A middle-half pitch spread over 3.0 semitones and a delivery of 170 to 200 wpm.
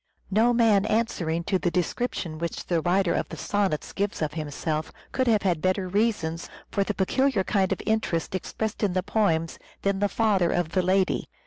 Yes: average, 3.8 semitones; average, 190 wpm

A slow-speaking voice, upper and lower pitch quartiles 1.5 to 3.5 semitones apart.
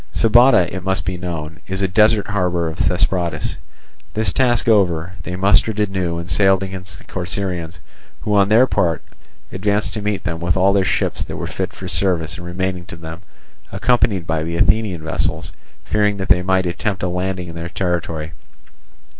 No: average, 180 wpm; average, 2.7 semitones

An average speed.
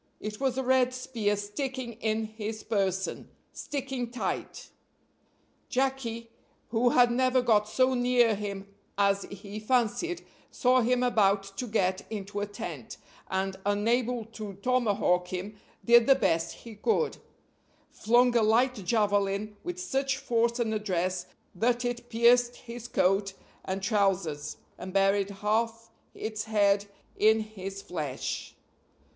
No: slow, 130 wpm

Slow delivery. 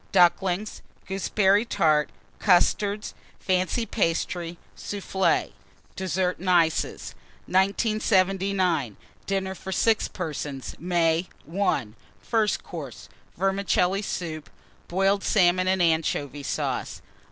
Yes: slow, 90 wpm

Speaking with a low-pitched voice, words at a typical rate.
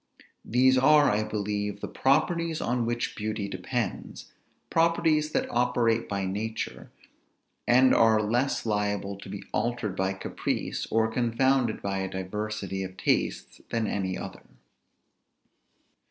No: low, 110 Hz; slow, 125 wpm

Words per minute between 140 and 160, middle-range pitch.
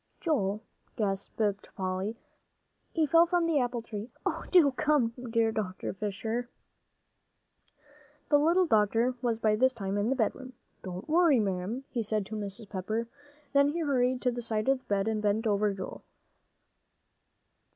No: average, 155 wpm; high, 225 Hz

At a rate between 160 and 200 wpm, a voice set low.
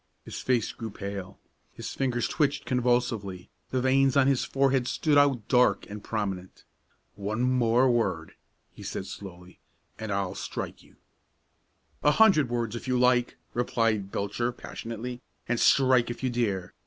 No: average, 150 wpm; low, 120 Hz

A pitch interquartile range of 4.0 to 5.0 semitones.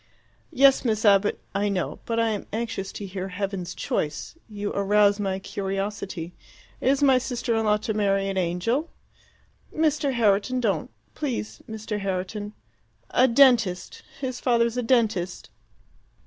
No: average, 3.6 semitones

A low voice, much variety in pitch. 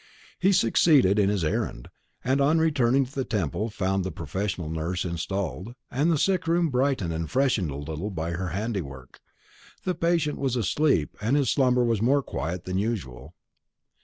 Yes: low, 105 Hz; wide, 7.8 semitones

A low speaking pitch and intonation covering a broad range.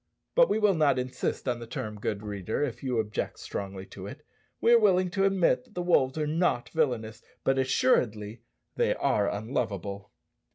Yes: low, 125 Hz; wide, 8.2 semitones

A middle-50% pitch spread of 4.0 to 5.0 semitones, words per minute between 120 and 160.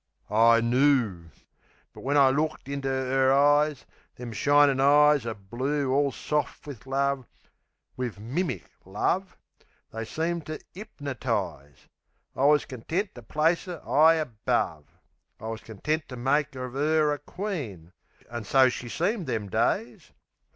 Yes: average, 4.3 semitones; average, 140 wpm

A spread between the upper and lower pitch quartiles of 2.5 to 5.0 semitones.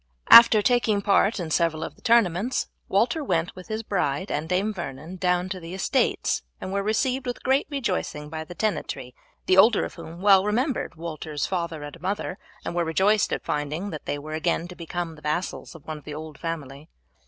Yes: average, 4.6 semitones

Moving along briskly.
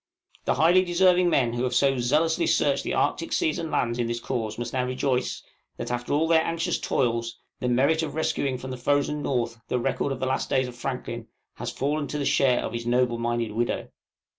Yes: fast, 215 wpm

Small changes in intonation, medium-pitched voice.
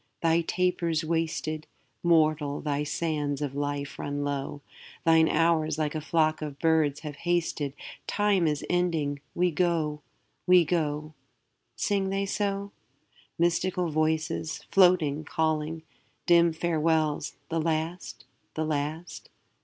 Yes: narrow, 2.3 semitones; medium, 160 Hz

